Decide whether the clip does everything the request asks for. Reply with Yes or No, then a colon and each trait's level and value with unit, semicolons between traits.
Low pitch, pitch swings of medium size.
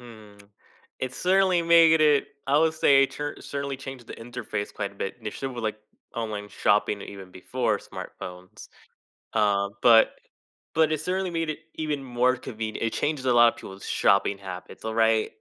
No: low, 120 Hz; wide, 6.1 semitones